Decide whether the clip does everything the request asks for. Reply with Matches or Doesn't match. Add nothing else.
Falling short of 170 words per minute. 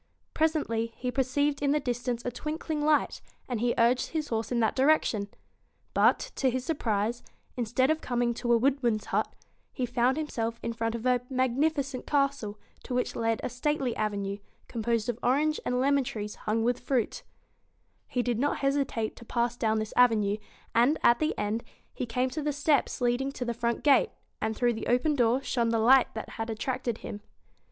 Doesn't match